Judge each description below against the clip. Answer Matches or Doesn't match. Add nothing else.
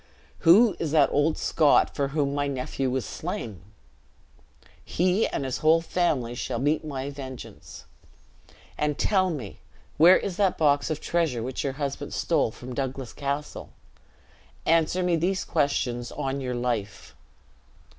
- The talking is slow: Doesn't match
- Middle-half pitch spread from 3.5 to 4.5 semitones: Matches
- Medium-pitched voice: Matches